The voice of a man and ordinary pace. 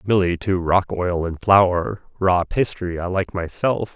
Yes: male; average, 165 wpm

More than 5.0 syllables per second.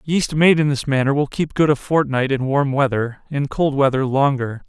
No: 4.9 syllables/s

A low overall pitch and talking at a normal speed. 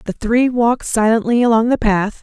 No: high, 230 Hz; average, 190 wpm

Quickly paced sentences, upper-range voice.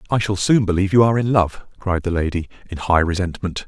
No: fast, 230 wpm; very low, 95 Hz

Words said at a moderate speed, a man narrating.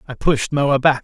No: fast, 235 wpm; male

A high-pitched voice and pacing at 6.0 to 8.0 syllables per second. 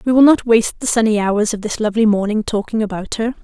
Yes: high, 220 Hz; 6.4 syllables/s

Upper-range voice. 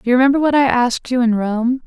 Yes: very high, 250 Hz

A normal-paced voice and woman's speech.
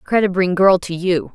No: fast, 225 wpm; female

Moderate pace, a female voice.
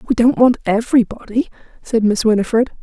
Yes: average, 150 wpm; female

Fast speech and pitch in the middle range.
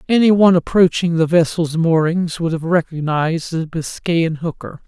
No: average, 150 wpm; medium, 165 Hz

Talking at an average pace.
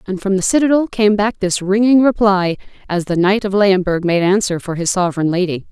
No: fast, 210 wpm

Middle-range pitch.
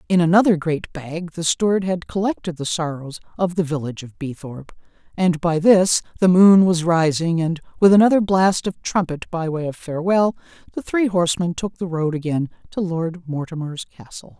Yes: medium, 170 Hz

